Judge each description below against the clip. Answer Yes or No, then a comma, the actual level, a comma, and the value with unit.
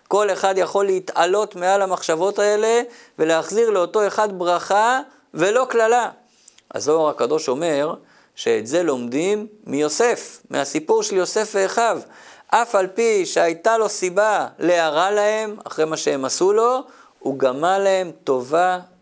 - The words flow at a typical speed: Yes, average, 130 wpm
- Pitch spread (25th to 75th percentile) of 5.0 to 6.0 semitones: No, average, 4.2 semitones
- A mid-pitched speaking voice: No, high, 205 Hz